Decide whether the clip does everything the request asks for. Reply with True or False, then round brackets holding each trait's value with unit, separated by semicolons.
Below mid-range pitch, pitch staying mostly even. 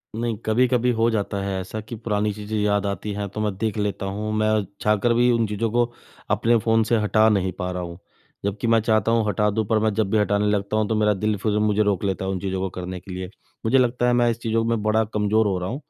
True (105 Hz; 1.9 semitones)